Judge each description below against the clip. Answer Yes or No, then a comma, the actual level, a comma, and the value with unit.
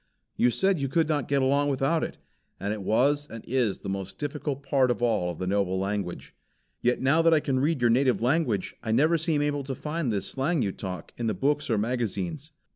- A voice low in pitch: Yes, low, 130 Hz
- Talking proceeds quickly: Yes, fast, 220 wpm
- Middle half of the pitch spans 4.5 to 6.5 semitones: Yes, wide, 5.5 semitones